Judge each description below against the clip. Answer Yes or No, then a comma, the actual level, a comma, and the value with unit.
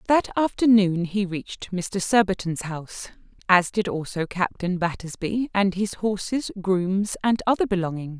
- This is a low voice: No, high, 195 Hz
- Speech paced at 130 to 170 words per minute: Yes, average, 140 wpm